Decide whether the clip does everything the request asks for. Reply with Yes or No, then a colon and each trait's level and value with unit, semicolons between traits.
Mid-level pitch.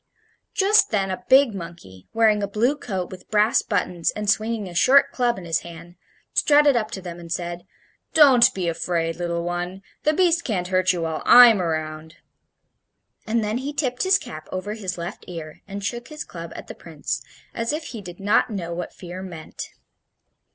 No: high, 195 Hz